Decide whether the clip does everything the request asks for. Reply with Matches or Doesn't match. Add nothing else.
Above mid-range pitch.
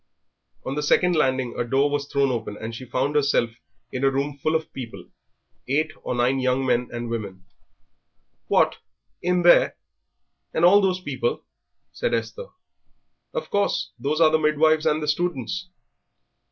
Doesn't match